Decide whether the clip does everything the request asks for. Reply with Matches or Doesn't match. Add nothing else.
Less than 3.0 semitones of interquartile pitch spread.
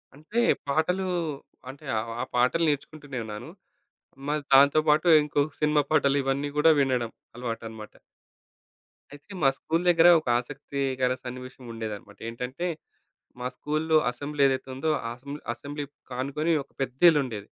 Doesn't match